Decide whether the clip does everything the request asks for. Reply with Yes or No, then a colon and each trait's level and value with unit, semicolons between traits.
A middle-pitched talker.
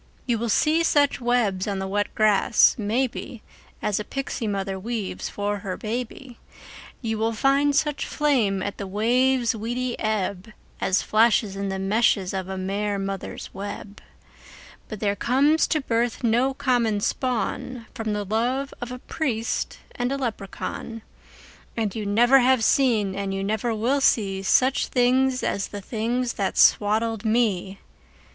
No: high, 225 Hz